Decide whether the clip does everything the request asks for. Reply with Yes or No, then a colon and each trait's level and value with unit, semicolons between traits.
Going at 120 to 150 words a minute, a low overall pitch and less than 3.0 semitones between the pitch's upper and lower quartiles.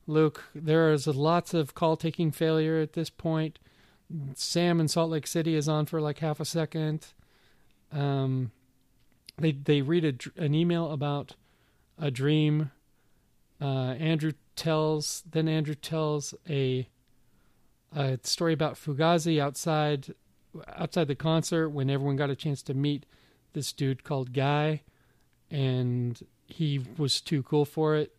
No: average, 140 wpm; medium, 150 Hz; narrow, 2.6 semitones